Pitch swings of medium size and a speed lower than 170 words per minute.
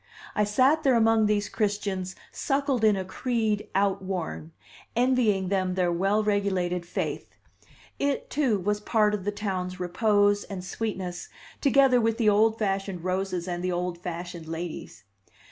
Yes: average, 3.3 semitones; average, 145 wpm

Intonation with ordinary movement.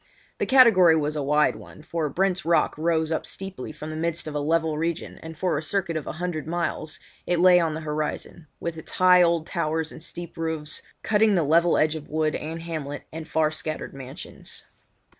No: narrow, 1.8 semitones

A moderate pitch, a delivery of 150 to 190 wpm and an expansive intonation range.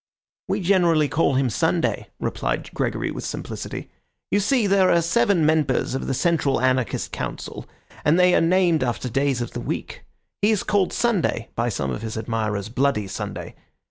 Yes: medium, 150 Hz; average, 175 wpm; wide, 7.0 semitones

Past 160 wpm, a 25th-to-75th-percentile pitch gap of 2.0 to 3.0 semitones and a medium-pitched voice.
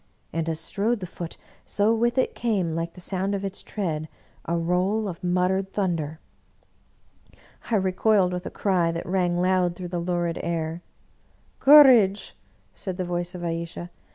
Yes: average, 170 wpm; narrow, 2.6 semitones; medium, 180 Hz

